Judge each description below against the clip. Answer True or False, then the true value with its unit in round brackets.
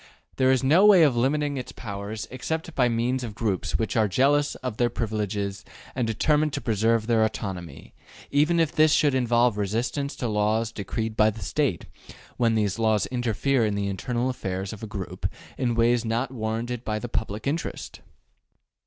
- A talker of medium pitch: False (115 Hz)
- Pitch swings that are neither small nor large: True (3.4 semitones)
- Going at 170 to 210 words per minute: True (180 wpm)